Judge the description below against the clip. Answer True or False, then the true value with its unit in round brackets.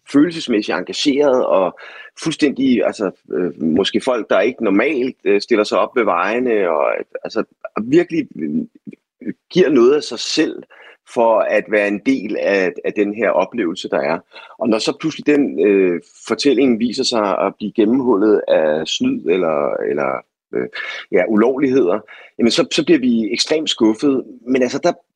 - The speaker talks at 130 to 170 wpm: True (150 wpm)